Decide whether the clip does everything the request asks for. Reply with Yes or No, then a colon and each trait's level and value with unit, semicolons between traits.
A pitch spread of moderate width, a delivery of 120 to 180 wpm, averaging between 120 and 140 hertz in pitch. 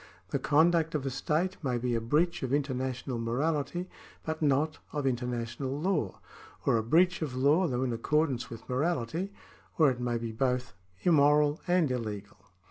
Yes: average, 4.4 semitones; average, 165 wpm; low, 135 Hz